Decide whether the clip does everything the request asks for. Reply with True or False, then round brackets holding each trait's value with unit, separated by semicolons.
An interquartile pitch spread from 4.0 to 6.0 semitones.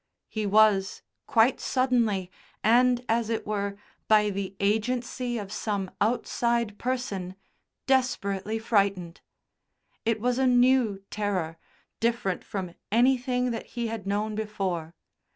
False (3.4 semitones)